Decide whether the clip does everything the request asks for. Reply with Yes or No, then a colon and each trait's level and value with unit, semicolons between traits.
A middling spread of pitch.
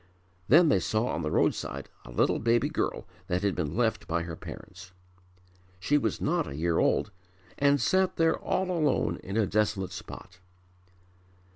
No: wide, 7.9 semitones